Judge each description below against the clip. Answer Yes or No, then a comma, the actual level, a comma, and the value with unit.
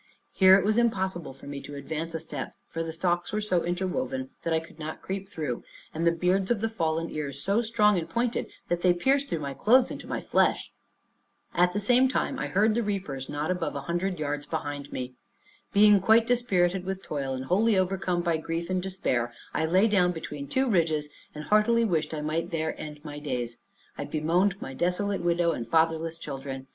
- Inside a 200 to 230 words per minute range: Yes, fast, 205 wpm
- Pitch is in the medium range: Yes, medium, 175 Hz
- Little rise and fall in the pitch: No, average, 4.6 semitones